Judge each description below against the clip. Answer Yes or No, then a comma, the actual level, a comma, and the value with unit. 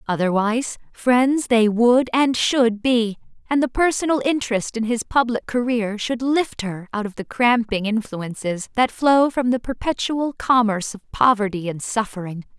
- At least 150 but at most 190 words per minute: Yes, average, 155 wpm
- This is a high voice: Yes, high, 230 Hz